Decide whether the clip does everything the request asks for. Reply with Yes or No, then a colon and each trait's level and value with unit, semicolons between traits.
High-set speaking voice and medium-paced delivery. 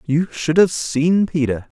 No: medium, 160 Hz; average, 170 wpm